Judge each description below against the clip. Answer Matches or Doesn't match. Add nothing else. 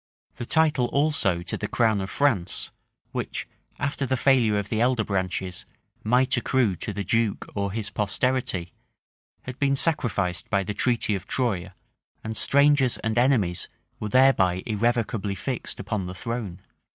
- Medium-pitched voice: Doesn't match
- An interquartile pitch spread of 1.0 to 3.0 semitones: Doesn't match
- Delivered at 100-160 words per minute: Matches